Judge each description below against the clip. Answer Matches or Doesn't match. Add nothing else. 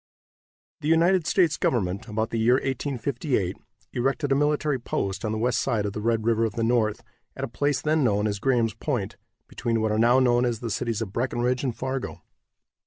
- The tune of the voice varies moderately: Matches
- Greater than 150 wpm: Matches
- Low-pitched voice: Matches